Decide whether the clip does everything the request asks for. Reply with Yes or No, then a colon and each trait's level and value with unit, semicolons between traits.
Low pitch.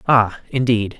Yes: low, 115 Hz